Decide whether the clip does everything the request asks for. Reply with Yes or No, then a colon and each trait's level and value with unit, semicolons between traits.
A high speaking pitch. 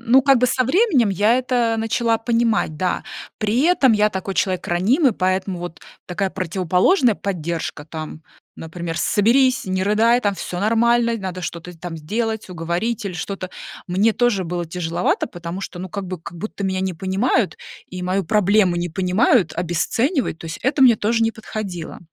Yes: high, 195 Hz